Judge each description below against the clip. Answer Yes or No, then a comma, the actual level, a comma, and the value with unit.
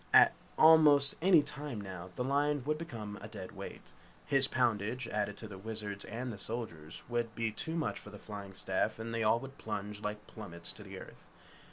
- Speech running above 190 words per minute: Yes, average, 200 wpm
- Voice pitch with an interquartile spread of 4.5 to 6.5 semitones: Yes, average, 4.8 semitones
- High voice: No, low, 110 Hz